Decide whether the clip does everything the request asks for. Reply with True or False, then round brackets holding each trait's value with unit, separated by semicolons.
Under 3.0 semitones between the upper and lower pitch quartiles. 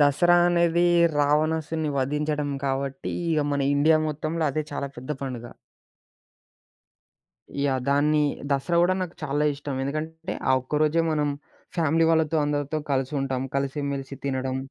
True (2.4 semitones)